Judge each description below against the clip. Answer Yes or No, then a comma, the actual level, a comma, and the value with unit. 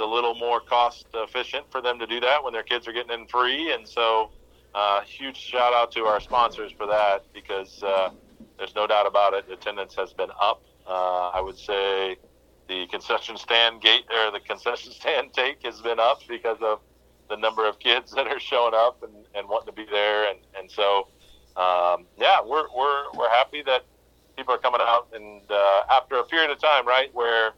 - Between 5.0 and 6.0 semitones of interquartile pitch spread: No, average, 3.4 semitones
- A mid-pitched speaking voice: No, low, 110 Hz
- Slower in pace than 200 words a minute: No, fast, 205 wpm